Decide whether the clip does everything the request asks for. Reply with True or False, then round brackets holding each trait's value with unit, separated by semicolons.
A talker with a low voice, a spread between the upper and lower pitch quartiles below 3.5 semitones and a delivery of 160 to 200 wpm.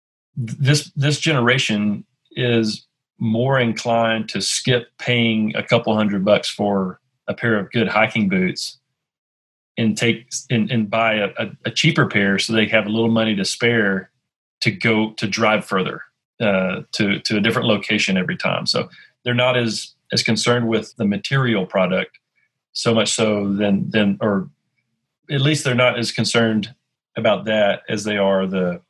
True (115 Hz; 2.7 semitones; 165 wpm)